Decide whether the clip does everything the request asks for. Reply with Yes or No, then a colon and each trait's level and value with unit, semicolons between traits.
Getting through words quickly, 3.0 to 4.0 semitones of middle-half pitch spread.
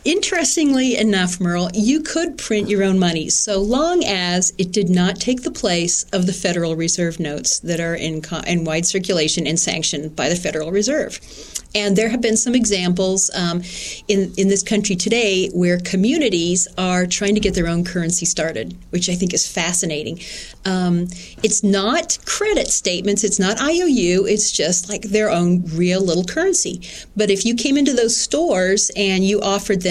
No: average, 180 wpm; average, 3.4 semitones